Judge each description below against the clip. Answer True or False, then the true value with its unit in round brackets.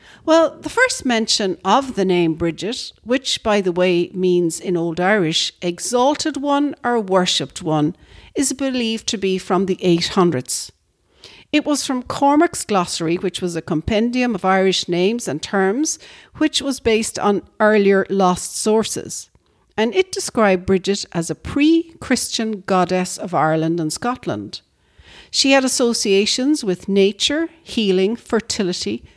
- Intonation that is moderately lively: False (6.0 semitones)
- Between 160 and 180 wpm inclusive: False (140 wpm)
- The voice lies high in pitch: True (200 Hz)